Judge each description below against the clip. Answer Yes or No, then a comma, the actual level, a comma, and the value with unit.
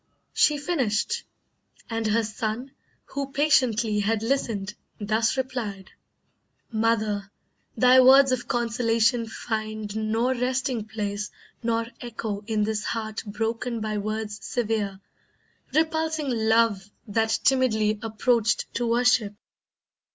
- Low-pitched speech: No, high, 225 Hz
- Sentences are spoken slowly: Yes, slow, 105 wpm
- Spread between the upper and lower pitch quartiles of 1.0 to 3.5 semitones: Yes, narrow, 2.6 semitones